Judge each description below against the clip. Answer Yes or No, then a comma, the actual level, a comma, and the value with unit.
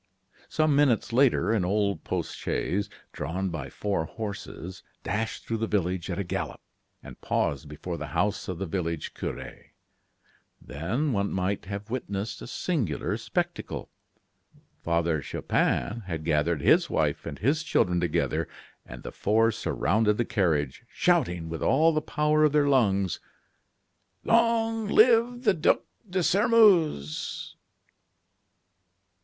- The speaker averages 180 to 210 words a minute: No, slow, 135 wpm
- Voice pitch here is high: No, low, 105 Hz